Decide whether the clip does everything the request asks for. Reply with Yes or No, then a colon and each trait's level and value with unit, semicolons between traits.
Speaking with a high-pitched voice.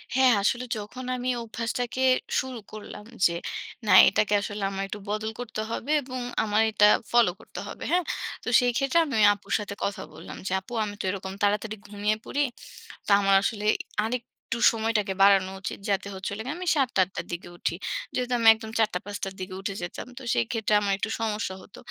Yes: high, 215 Hz